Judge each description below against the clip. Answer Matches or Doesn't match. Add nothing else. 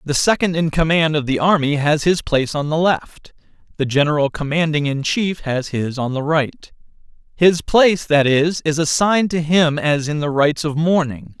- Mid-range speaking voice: Matches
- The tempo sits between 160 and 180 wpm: Doesn't match